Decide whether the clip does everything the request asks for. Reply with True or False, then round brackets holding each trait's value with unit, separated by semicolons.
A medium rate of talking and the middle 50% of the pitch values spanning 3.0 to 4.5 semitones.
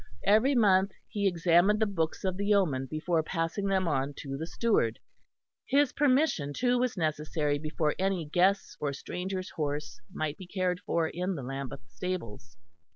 False (160 wpm; 5.0 semitones)